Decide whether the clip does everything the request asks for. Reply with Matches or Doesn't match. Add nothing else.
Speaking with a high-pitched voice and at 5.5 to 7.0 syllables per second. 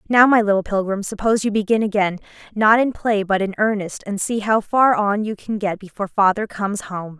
Matches